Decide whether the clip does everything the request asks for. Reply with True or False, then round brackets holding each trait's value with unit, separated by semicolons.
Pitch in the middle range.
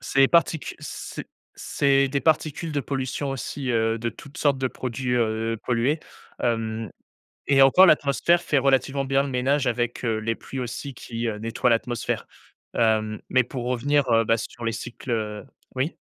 False (125 Hz)